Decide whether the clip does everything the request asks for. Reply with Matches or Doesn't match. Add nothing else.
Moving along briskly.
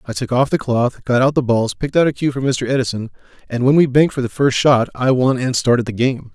Matches